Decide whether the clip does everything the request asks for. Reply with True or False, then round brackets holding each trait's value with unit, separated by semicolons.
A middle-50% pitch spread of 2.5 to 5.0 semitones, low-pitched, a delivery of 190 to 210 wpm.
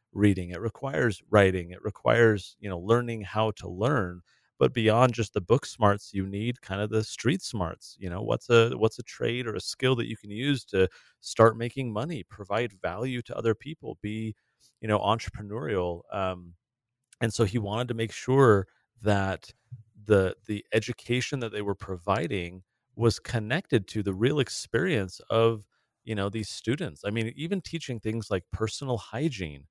False (3.2 semitones; 110 Hz; 175 wpm)